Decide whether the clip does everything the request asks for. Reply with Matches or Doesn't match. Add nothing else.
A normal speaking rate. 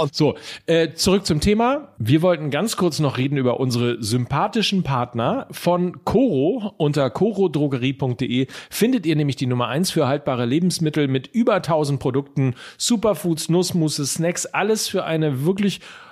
Matches